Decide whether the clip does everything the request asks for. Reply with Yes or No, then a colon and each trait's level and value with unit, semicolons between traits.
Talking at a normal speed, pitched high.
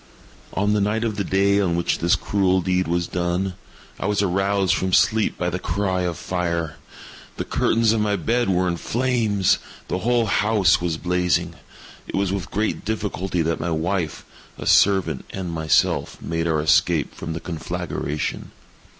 No: average, 170 wpm; very low, 95 Hz